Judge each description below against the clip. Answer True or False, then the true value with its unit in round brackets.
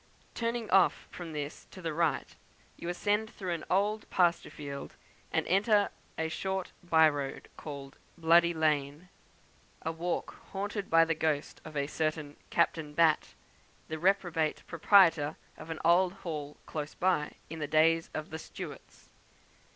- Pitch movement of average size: True (3.0 semitones)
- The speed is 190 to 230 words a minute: False (150 wpm)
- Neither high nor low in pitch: True (165 Hz)